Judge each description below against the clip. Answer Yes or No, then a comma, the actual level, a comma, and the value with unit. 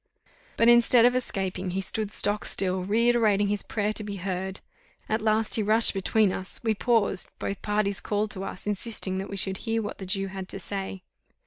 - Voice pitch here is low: No, high, 205 Hz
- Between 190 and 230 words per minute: Yes, average, 200 wpm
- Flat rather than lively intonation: Yes, narrow, 2.3 semitones